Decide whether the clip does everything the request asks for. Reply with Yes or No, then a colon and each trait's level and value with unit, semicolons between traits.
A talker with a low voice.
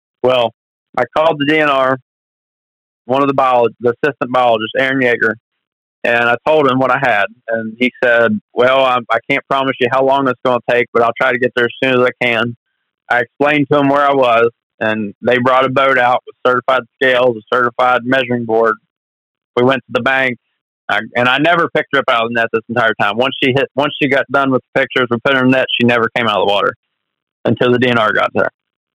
Yes: low, 125 Hz